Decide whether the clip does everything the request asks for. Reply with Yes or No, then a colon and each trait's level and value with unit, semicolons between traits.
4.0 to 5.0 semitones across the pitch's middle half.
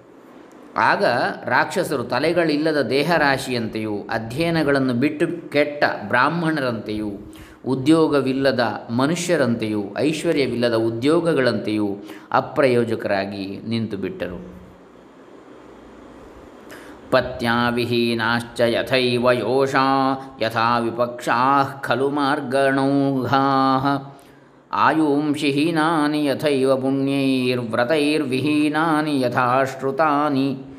No: average, 3.3 semitones